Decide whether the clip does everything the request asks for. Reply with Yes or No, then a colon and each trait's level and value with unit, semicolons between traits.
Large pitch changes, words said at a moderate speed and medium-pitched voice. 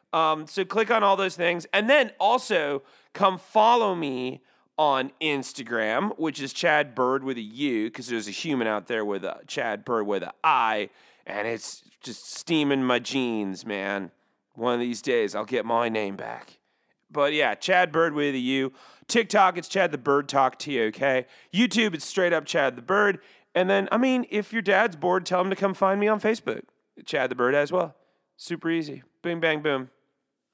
Yes: wide, 6.8 semitones; average, 195 wpm; medium, 160 Hz